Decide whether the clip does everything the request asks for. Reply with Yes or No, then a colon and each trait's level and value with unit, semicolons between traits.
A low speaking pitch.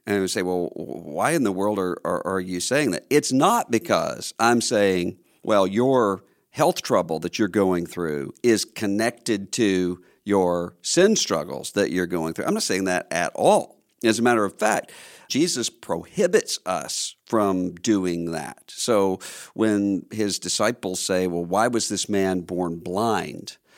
Yes: very low, 95 Hz